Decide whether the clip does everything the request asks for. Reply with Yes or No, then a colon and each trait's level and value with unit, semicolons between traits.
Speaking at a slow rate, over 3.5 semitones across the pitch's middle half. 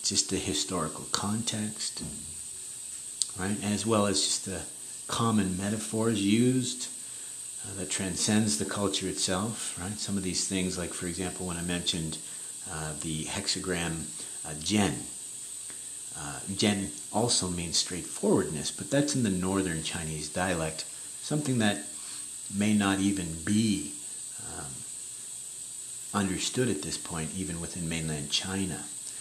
Yes: slow, 125 wpm; average, 3.9 semitones